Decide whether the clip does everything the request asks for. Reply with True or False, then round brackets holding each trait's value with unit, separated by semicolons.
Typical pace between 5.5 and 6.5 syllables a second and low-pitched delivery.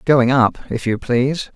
False (4.3 syllables/s; 130 Hz)